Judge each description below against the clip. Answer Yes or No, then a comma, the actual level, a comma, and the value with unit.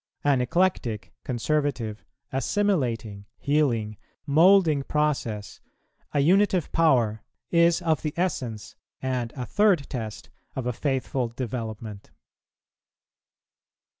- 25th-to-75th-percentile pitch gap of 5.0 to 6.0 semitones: Yes, wide, 5.4 semitones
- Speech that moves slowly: Yes, slow, 95 wpm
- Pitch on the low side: Yes, low, 130 Hz